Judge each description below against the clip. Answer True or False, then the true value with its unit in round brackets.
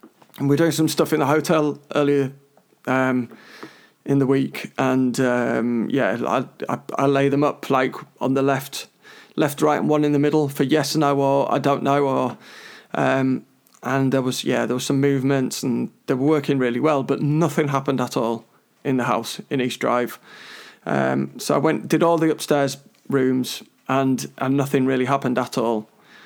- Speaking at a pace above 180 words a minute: True (195 wpm)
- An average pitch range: False (2.3 semitones)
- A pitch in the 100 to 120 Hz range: False (140 Hz)